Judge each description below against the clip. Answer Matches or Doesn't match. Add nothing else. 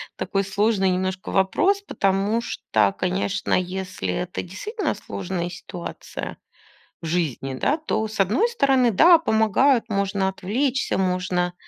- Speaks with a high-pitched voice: Matches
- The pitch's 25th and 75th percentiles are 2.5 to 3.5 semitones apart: Doesn't match